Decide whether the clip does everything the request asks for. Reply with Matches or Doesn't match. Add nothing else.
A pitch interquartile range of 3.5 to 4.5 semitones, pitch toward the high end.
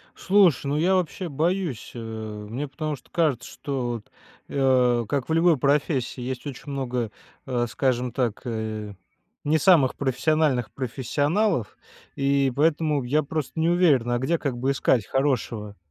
Doesn't match